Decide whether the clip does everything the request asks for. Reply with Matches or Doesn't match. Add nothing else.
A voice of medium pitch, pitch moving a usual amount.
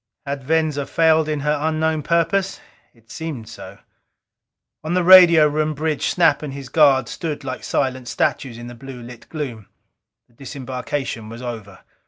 Matches